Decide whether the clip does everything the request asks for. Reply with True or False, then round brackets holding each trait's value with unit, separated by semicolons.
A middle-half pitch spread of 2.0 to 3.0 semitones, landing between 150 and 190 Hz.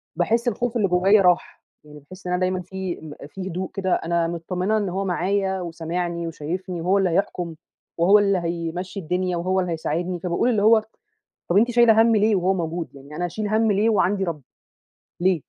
True (2.7 semitones; 185 Hz)